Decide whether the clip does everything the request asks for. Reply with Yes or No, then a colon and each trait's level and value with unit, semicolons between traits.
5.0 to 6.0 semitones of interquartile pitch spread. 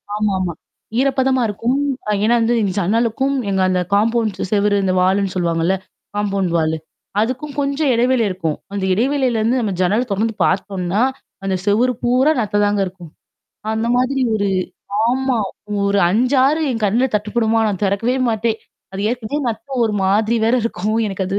No: average, 4.0 semitones